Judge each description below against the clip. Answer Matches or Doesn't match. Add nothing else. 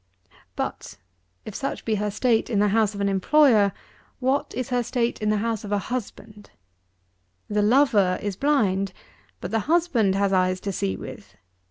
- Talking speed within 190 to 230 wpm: Doesn't match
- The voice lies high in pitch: Matches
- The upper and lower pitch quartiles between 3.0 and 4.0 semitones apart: Matches